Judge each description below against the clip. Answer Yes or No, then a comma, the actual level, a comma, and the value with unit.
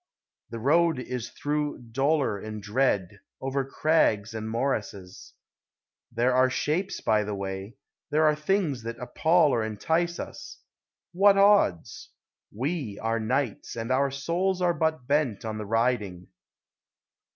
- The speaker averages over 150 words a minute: No, slow, 135 wpm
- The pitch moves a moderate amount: No, wide, 5.9 semitones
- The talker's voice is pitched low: Yes, low, 130 Hz